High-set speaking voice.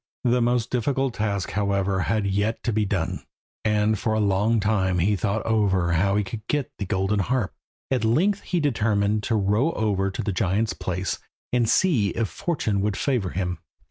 No: low, 105 Hz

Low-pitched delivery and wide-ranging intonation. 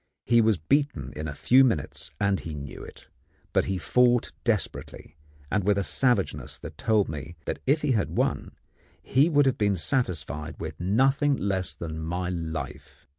Yes: very low, 95 Hz; wide, 7.7 semitones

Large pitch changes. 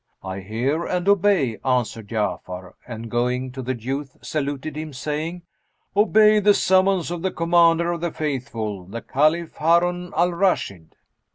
Yes: wide, 6.4 semitones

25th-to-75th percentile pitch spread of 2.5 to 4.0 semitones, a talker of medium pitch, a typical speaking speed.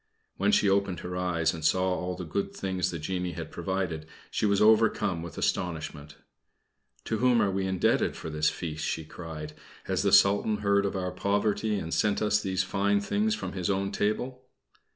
No: average, 2.9 semitones; very low, 95 Hz; average, 190 wpm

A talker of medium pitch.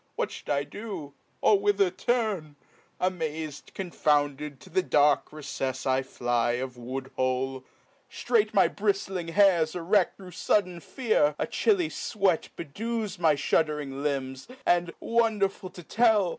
Yes: medium, 165 Hz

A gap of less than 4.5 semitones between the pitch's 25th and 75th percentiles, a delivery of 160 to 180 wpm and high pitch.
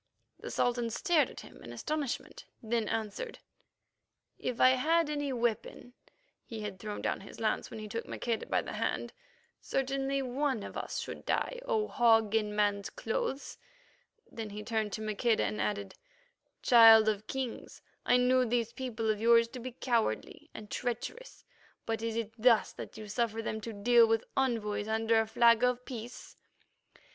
Yes: narrow, 2.6 semitones; average, 170 wpm; high, 230 Hz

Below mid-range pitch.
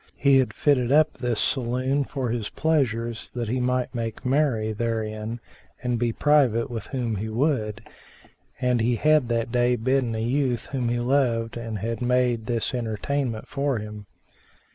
Yes: low, 120 Hz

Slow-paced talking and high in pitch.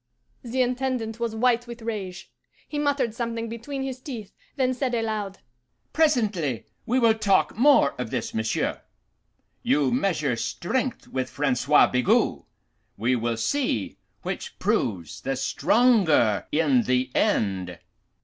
Yes: slow, 130 wpm; high, 215 Hz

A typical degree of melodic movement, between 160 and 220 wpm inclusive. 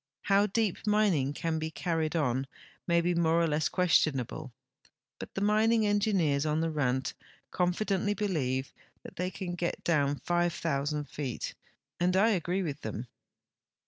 No: average, 4.6 semitones; average, 145 wpm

